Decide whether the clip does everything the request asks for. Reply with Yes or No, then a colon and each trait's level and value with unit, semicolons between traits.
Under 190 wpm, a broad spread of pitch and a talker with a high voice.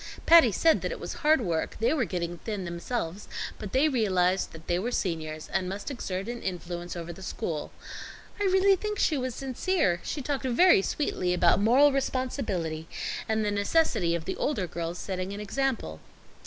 Yes: average, 180 wpm; wide, 7.4 semitones; high, 205 Hz